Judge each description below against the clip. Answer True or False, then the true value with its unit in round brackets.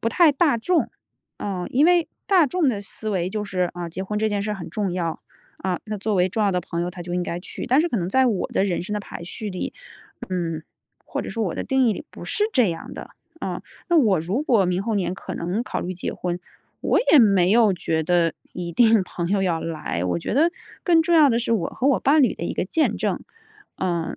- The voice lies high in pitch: True (200 Hz)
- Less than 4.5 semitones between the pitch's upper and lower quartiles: False (5.3 semitones)